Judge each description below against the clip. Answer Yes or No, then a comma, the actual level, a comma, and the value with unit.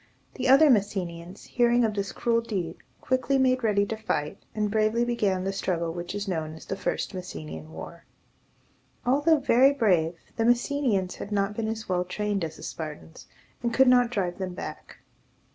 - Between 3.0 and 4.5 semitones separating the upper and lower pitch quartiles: No, average, 5.1 semitones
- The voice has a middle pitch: No, high, 205 Hz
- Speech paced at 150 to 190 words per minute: Yes, average, 180 wpm